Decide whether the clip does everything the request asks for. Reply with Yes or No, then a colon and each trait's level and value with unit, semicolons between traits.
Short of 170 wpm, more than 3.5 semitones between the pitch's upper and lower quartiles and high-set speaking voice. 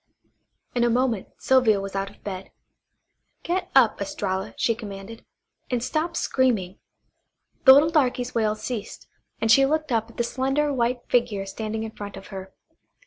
Yes: average, 160 wpm; average, 4.4 semitones; high, 230 Hz